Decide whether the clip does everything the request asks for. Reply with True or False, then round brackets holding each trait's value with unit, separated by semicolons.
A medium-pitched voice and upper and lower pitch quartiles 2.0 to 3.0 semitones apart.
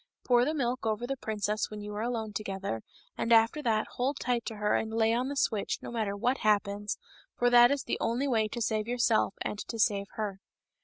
False (225 Hz; 2.6 semitones)